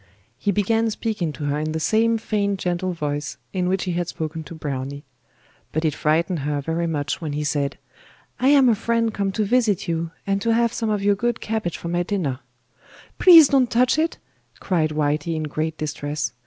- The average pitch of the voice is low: No, medium, 175 Hz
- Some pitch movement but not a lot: No, wide, 6.2 semitones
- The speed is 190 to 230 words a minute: Yes, average, 200 wpm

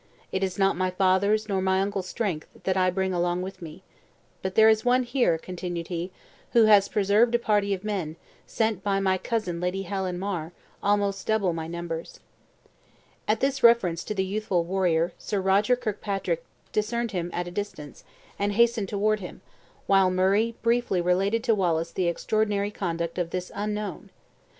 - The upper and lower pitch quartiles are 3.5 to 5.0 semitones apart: No, average, 3.0 semitones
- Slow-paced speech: No, average, 175 wpm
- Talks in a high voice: Yes, high, 195 Hz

